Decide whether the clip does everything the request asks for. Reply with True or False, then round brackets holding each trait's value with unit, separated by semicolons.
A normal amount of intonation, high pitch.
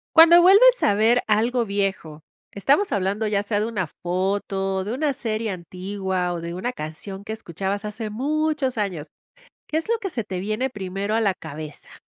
True (4.5 semitones; 205 Hz)